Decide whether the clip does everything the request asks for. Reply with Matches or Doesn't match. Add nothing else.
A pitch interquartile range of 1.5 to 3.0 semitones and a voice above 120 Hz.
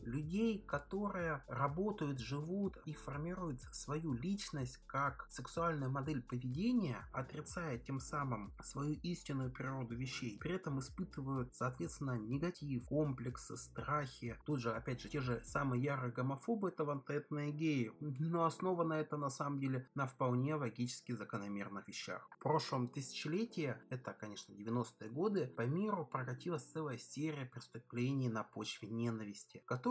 Doesn't match